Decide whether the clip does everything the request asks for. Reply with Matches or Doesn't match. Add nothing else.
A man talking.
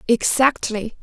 Doesn't match